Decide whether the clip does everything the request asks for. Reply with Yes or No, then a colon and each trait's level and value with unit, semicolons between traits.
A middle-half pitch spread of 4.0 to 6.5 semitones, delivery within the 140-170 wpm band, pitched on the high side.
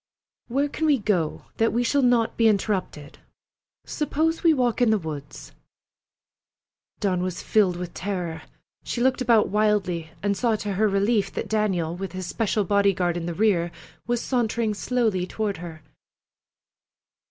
Yes: average, 4.6 semitones; average, 155 wpm; high, 205 Hz